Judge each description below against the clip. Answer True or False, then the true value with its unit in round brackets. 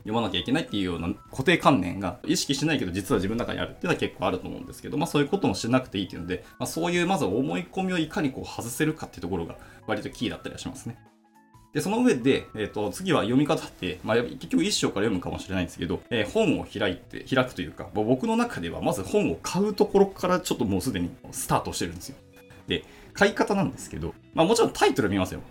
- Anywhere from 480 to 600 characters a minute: True (540 characters per minute)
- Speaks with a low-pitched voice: True (130 Hz)